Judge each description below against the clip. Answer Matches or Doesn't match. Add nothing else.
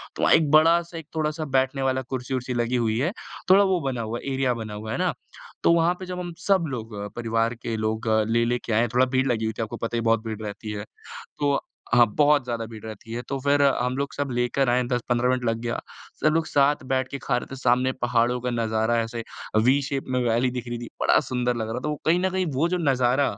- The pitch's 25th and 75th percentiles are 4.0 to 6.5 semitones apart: Doesn't match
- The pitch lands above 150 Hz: Doesn't match